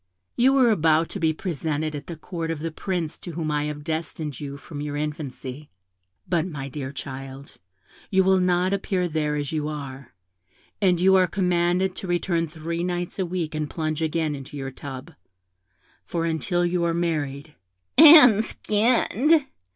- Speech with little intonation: No, average, 3.4 semitones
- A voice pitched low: No, medium, 165 Hz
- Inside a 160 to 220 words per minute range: Yes, average, 170 wpm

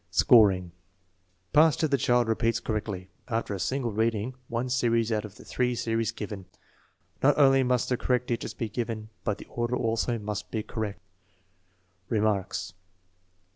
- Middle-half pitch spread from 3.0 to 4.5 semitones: No, narrow, 2.5 semitones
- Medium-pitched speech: No, low, 115 Hz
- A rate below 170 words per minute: Yes, average, 155 wpm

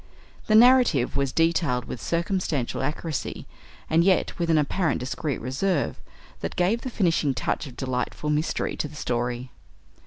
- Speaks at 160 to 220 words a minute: No, average, 150 wpm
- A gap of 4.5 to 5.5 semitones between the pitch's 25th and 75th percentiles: Yes, average, 5.2 semitones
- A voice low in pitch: No, medium, 155 Hz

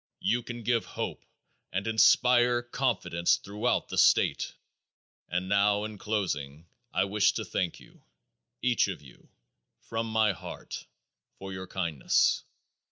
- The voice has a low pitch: Yes, low, 105 Hz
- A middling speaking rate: No, slow, 130 wpm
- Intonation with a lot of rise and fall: No, average, 3.6 semitones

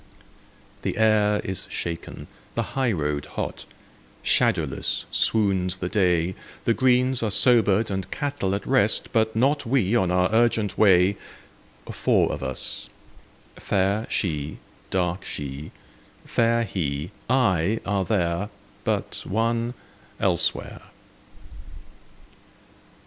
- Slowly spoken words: Yes, slow, 105 wpm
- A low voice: Yes, low, 100 Hz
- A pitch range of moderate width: Yes, average, 4.2 semitones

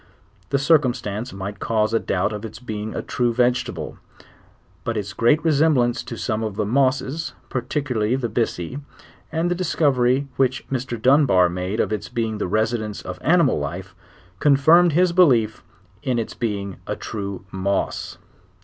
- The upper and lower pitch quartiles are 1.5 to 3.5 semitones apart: No, average, 4.7 semitones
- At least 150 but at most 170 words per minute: Yes, average, 160 wpm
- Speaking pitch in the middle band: No, low, 120 Hz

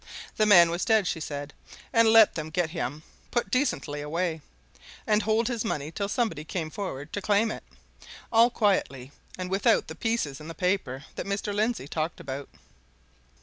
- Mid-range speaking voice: Yes, medium, 180 Hz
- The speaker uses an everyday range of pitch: No, wide, 5.9 semitones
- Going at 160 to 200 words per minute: Yes, average, 175 wpm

